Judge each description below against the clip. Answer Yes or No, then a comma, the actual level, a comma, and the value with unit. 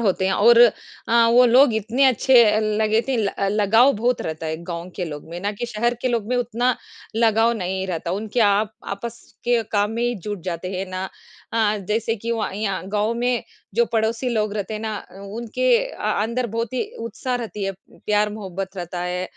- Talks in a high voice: Yes, high, 220 Hz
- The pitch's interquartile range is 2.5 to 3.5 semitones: Yes, average, 3.2 semitones